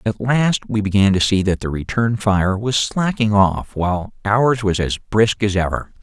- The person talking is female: No, male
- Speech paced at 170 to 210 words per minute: Yes, average, 200 wpm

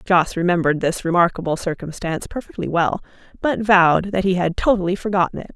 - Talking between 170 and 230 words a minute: No, average, 160 wpm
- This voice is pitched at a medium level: Yes, medium, 180 Hz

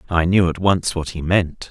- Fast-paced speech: Yes, fast, 245 wpm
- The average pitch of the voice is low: Yes, very low, 90 Hz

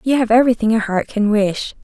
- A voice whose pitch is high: Yes, high, 225 Hz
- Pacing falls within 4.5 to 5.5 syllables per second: No, 6.0 syllables/s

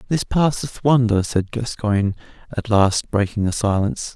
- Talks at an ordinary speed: Yes, average, 145 wpm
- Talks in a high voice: No, low, 110 Hz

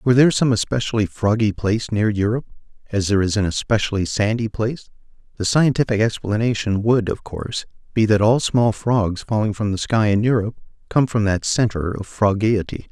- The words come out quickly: No, average, 175 wpm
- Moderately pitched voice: No, low, 110 Hz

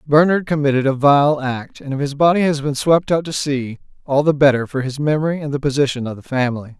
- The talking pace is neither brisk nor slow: No, fast, 240 wpm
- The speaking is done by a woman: No, male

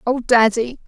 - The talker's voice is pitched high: Yes, high, 235 Hz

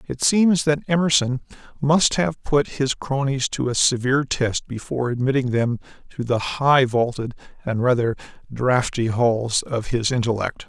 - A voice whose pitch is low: Yes, low, 130 Hz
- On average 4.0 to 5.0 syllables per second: Yes, 4.5 syllables/s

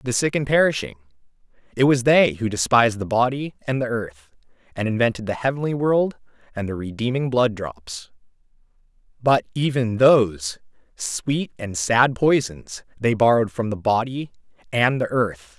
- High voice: No, low, 120 Hz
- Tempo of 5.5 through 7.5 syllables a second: No, 4.8 syllables/s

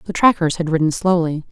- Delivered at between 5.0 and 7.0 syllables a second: Yes, 6.1 syllables/s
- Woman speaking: Yes, female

